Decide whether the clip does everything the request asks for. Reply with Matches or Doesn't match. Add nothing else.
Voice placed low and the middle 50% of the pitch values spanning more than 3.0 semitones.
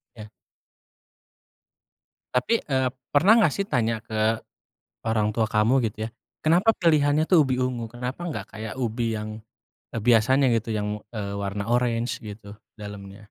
Matches